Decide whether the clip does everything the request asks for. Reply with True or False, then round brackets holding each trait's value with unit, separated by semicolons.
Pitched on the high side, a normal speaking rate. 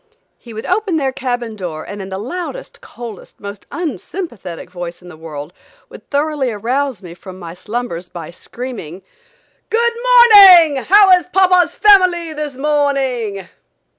True (250 Hz; 145 wpm)